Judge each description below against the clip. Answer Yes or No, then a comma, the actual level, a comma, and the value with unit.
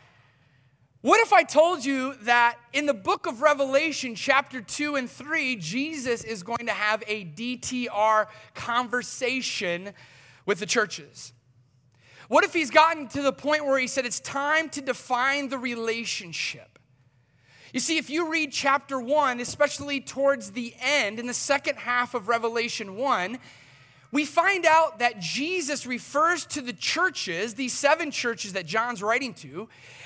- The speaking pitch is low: No, very high, 250 Hz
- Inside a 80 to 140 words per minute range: No, average, 150 wpm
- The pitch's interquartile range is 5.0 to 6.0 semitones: Yes, wide, 5.4 semitones